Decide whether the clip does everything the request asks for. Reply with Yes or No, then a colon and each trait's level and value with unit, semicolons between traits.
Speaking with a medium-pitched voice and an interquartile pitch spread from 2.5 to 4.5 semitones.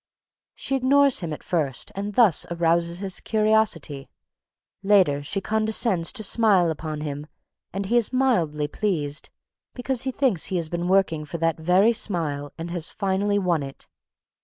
No: medium, 180 Hz; average, 5.3 semitones